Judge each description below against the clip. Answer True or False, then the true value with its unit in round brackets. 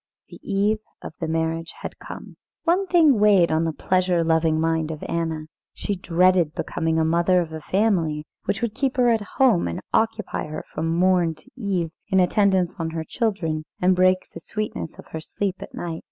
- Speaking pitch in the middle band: True (180 Hz)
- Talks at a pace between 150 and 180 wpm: False (195 wpm)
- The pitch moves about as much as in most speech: True (4.0 semitones)